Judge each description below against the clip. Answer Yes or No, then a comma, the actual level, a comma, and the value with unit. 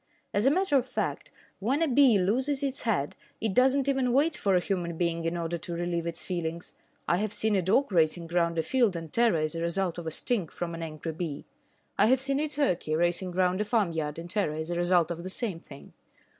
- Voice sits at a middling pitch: Yes, medium, 180 Hz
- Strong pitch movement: Yes, wide, 6.1 semitones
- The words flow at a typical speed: No, fast, 240 wpm